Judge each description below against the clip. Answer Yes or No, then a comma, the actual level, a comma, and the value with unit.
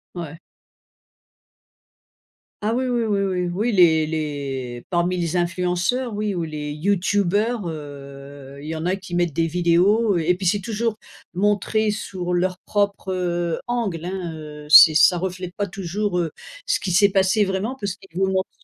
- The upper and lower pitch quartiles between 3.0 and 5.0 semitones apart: Yes, average, 3.6 semitones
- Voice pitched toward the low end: No, medium, 180 Hz